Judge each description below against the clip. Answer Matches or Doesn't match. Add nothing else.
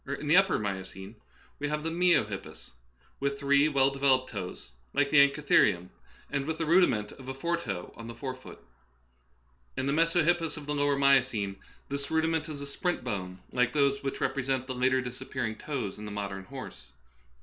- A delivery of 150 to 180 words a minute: Doesn't match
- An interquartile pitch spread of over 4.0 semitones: Matches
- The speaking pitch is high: Doesn't match